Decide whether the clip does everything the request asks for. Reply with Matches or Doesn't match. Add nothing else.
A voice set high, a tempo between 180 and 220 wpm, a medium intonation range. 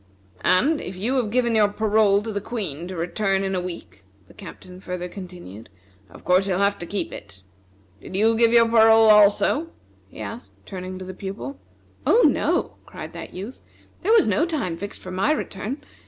Matches